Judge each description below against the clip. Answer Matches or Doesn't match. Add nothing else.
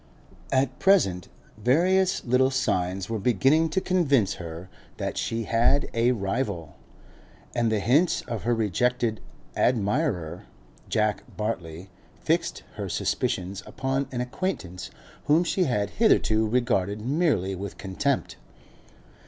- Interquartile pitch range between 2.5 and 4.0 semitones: Doesn't match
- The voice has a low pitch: Matches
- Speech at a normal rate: Doesn't match